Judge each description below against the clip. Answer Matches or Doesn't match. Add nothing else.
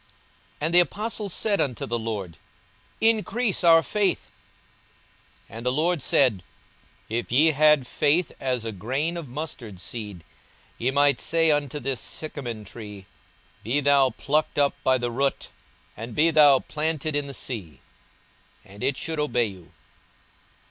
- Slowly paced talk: Doesn't match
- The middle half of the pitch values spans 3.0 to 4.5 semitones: Doesn't match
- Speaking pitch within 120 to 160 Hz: Matches